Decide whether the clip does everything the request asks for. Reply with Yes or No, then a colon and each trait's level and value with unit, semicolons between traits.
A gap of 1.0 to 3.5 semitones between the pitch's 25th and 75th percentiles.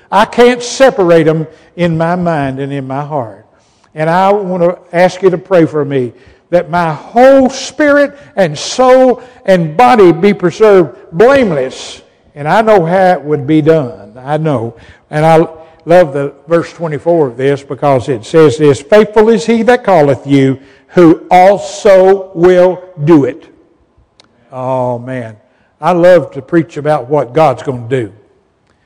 No: average, 5.1 semitones